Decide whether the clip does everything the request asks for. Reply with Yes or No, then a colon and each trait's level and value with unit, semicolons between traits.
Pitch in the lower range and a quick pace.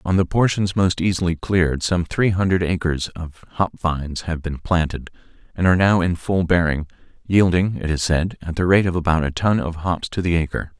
Yes: very low, 85 Hz; fast, 210 wpm